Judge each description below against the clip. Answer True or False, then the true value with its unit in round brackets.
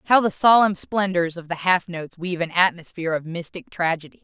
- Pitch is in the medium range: True (175 Hz)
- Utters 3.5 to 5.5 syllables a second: False (5.9 syllables/s)